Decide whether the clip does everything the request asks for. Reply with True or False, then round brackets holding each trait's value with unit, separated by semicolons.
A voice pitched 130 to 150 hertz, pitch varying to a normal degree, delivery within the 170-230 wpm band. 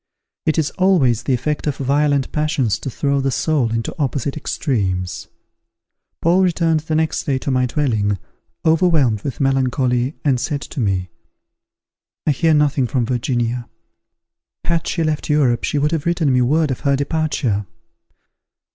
False (140 Hz; 4.0 semitones; 155 wpm)